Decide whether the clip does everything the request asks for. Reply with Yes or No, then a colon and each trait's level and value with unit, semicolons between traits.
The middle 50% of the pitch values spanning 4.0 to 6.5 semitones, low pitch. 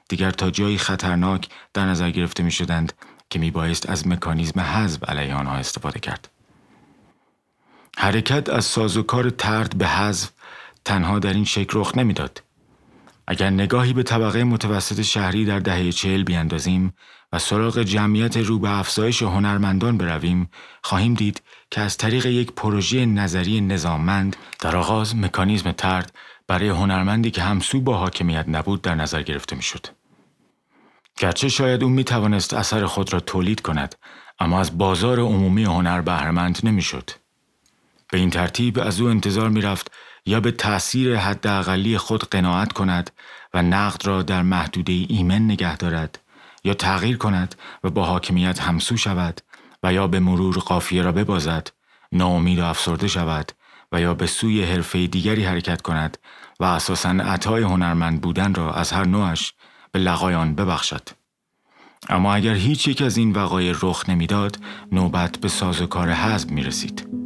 No: average, 3.2 semitones; very low, 95 Hz